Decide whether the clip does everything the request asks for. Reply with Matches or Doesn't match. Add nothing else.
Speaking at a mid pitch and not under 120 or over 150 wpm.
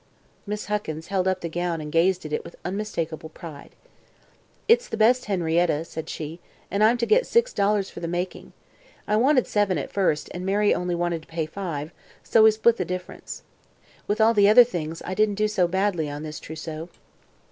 Doesn't match